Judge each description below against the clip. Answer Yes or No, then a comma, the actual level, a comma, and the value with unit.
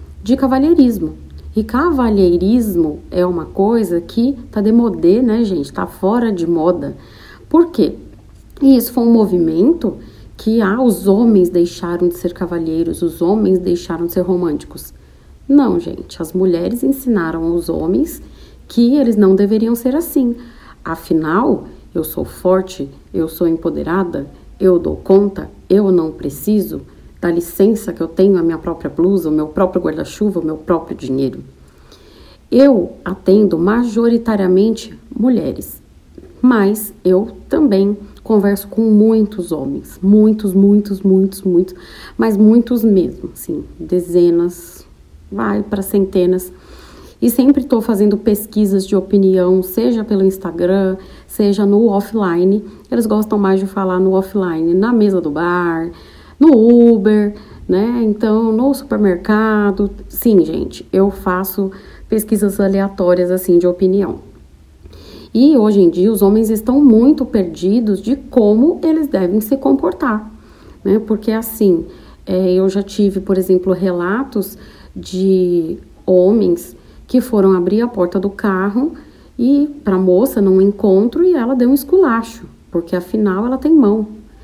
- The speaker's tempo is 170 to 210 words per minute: No, average, 135 wpm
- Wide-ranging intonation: No, average, 4.0 semitones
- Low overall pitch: No, high, 195 Hz